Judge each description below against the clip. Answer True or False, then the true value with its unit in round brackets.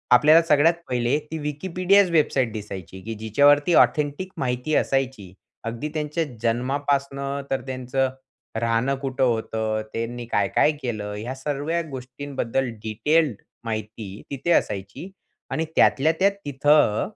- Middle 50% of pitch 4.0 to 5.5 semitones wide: True (4.5 semitones)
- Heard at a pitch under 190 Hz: True (135 Hz)